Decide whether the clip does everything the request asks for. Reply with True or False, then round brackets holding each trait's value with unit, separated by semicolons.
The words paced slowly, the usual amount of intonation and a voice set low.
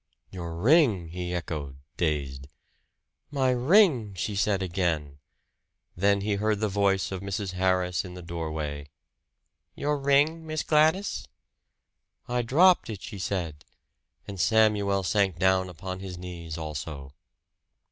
True (125 wpm; 4.6 semitones; 95 Hz)